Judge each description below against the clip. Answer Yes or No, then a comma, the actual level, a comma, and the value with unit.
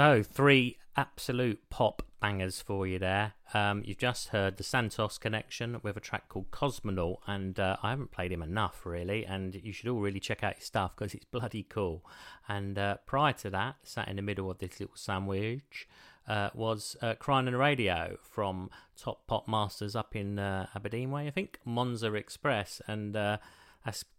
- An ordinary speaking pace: Yes, average, 190 wpm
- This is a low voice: Yes, low, 105 Hz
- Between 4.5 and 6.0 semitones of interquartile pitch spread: No, average, 3.2 semitones